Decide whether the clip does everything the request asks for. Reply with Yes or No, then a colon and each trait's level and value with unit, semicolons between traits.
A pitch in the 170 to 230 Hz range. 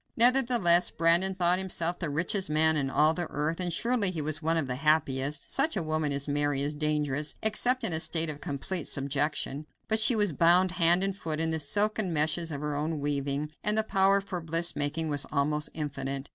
No: medium, 160 Hz